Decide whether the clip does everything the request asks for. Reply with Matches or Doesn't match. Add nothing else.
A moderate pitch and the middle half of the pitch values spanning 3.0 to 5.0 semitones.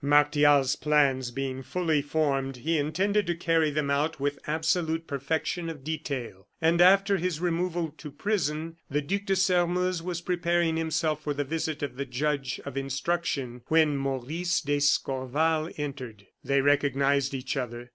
Matches